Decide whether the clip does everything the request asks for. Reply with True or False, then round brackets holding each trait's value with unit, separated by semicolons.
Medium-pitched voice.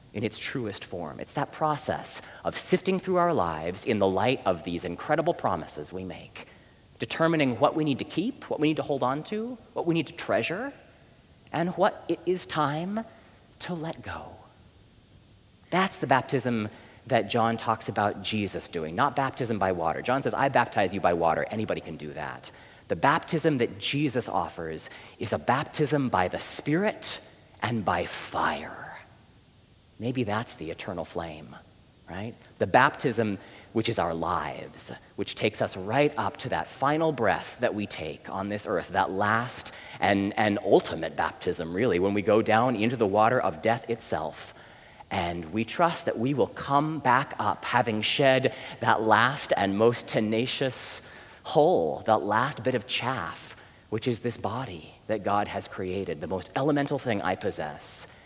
False (115 Hz)